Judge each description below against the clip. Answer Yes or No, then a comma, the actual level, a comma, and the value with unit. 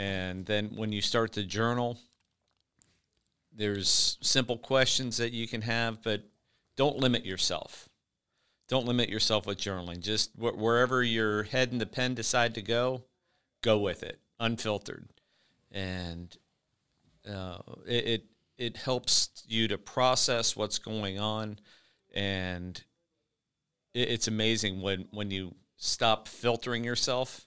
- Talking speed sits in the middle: No, slow, 130 wpm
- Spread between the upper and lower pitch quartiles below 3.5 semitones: Yes, average, 3.0 semitones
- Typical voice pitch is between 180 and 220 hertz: No, low, 115 Hz